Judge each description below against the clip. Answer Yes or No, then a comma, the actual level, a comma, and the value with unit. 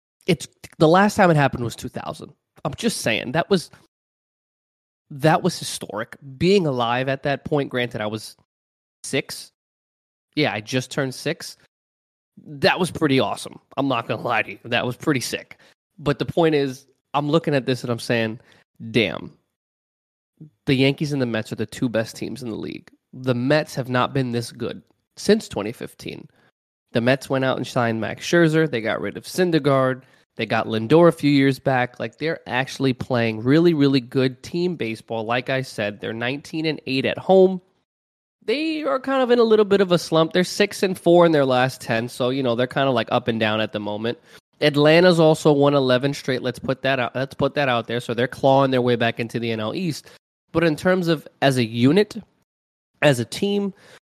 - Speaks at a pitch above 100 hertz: Yes, low, 135 Hz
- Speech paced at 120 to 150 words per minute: No, average, 200 wpm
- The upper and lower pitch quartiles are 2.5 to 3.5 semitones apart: No, average, 5.0 semitones